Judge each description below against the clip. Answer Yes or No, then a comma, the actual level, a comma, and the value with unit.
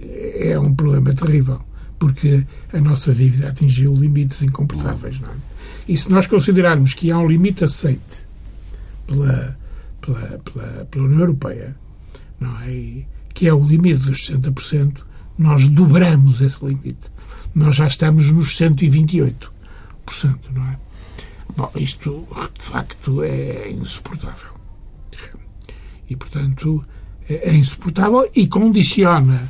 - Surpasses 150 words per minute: No, slow, 120 wpm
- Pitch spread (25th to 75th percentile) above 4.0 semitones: No, average, 3.6 semitones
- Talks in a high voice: No, low, 135 Hz